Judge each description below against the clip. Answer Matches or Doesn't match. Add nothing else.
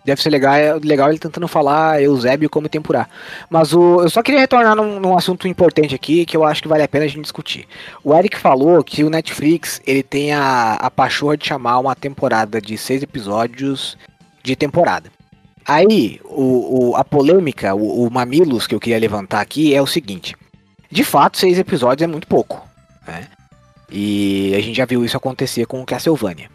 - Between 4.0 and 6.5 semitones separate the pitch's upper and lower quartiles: Matches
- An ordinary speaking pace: Doesn't match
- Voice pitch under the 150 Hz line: Matches